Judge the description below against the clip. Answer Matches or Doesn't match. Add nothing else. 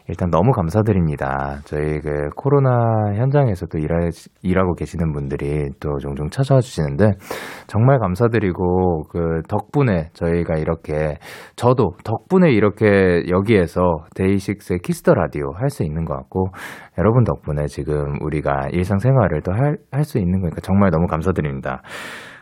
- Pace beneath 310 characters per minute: Doesn't match